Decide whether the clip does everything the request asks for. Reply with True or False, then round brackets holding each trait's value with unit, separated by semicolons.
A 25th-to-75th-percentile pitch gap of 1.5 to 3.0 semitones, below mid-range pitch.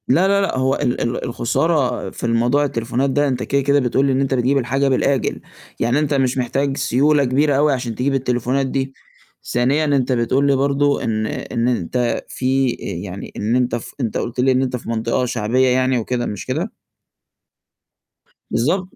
True (2.4 semitones; 130 Hz)